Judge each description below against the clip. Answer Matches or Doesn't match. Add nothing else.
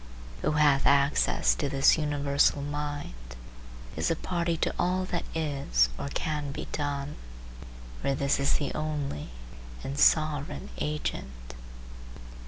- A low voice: Doesn't match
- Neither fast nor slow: Doesn't match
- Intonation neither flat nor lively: Doesn't match